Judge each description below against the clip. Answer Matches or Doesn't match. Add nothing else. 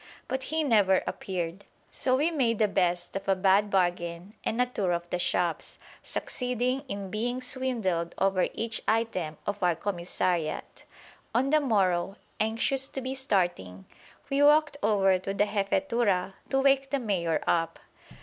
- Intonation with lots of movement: Matches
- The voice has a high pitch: Matches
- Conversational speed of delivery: Matches